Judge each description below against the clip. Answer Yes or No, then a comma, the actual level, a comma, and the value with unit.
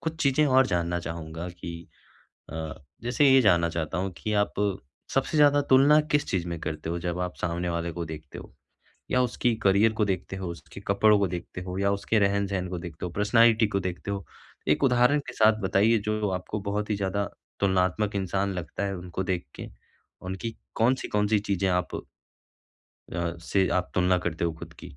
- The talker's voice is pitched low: Yes, very low, 95 Hz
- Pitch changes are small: No, average, 3.6 semitones